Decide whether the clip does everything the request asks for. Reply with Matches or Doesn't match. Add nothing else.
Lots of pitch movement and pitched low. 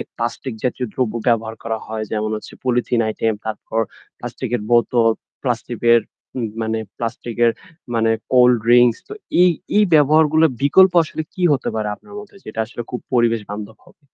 Doesn't match